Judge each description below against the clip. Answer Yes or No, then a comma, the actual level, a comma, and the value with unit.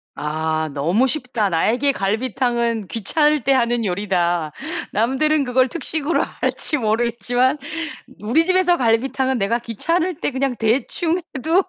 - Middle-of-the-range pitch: No, high, 245 Hz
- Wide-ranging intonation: No, average, 5.0 semitones